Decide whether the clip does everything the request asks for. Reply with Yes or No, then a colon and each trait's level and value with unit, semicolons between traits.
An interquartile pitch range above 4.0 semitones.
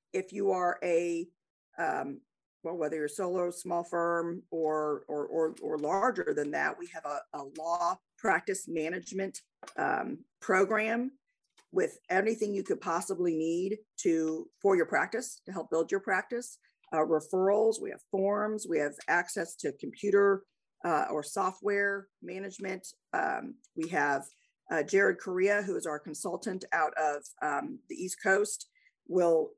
Yes: average, 4.4 semitones